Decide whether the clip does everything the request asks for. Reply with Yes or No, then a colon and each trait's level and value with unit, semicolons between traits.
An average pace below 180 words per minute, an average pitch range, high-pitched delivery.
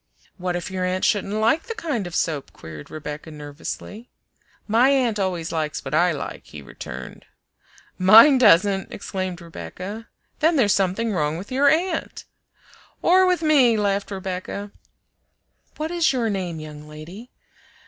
No: average, 150 wpm; wide, 6.4 semitones; high, 195 Hz